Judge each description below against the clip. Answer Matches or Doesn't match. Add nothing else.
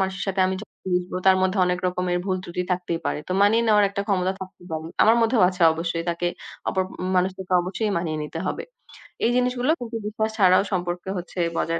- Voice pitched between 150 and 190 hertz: Matches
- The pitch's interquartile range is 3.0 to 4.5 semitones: Doesn't match